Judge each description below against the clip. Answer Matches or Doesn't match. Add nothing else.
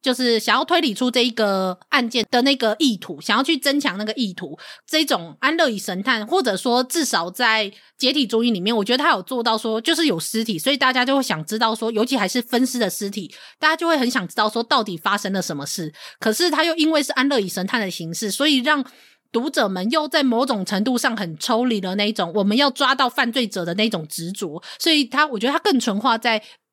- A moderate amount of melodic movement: Matches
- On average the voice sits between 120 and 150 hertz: Doesn't match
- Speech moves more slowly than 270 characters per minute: Doesn't match